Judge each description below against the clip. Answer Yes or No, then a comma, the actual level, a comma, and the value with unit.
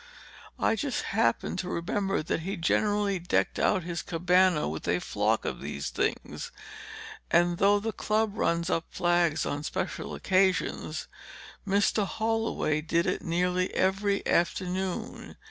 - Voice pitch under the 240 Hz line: Yes, medium, 185 Hz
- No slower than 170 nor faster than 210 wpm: No, slow, 135 wpm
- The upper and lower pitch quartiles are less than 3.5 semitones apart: Yes, average, 2.9 semitones